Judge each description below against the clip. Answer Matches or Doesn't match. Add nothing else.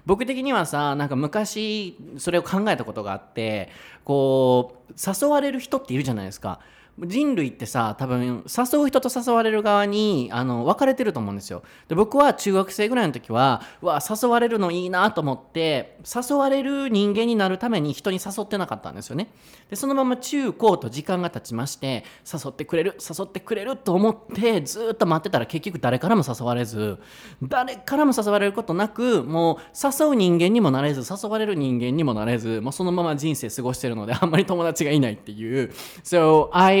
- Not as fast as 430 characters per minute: Matches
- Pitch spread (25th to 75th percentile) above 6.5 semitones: Matches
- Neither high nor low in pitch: Matches